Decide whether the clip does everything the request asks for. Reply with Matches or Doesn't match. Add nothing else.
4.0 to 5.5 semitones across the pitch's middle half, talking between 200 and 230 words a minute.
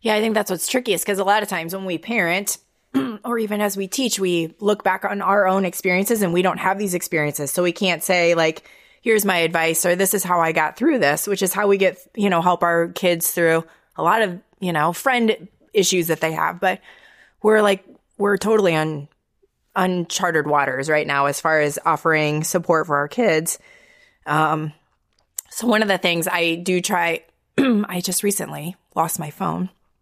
Doesn't match